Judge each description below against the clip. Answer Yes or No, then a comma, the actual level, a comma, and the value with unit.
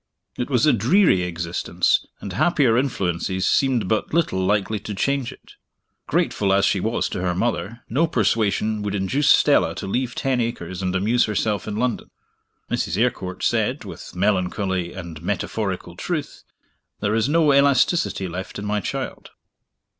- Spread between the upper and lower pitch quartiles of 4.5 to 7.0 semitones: Yes, average, 4.9 semitones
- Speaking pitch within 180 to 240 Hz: No, low, 105 Hz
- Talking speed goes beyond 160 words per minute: No, average, 155 wpm